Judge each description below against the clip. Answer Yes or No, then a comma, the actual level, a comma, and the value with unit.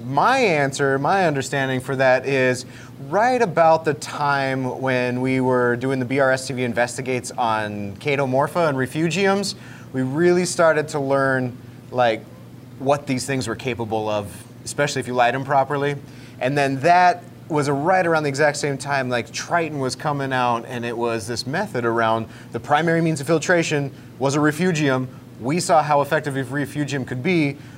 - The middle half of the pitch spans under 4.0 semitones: Yes, average, 3.0 semitones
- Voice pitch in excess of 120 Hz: Yes, low, 135 Hz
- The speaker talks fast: No, average, 165 wpm